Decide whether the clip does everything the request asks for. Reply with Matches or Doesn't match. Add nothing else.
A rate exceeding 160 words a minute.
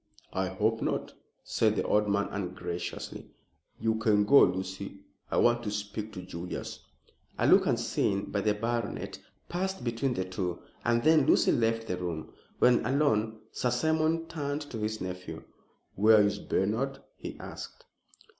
Doesn't match